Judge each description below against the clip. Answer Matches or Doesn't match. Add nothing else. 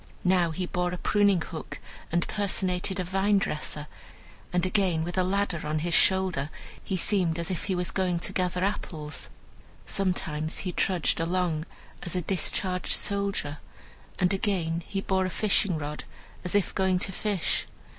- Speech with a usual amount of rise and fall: Doesn't match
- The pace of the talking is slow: Doesn't match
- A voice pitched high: Doesn't match